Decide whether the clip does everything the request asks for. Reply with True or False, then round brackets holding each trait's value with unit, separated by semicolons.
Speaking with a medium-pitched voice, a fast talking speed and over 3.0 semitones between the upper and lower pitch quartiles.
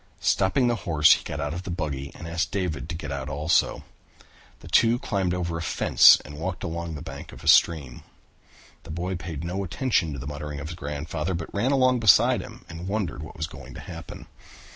False (85 Hz; 215 wpm; 3.7 semitones)